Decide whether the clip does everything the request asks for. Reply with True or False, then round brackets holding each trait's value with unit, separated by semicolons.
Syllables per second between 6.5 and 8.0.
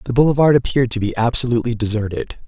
True (7.4 syllables/s)